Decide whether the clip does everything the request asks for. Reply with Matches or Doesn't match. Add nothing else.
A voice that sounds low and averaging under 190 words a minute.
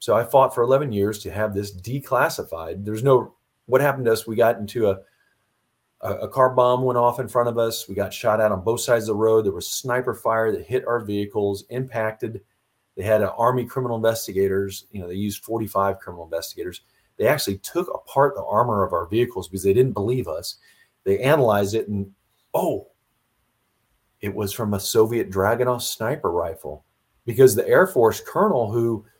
Doesn't match